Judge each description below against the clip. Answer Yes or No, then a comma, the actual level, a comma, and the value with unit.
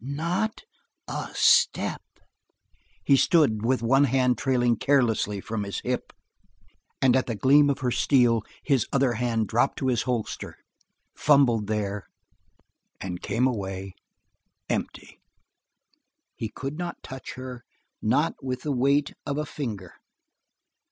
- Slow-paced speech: Yes, slow, 130 wpm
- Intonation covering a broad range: No, average, 3.7 semitones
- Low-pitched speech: Yes, low, 125 Hz